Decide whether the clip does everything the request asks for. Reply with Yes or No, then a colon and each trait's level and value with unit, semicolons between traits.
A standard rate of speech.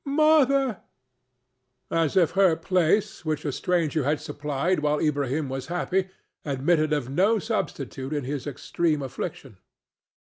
No: slow, 130 wpm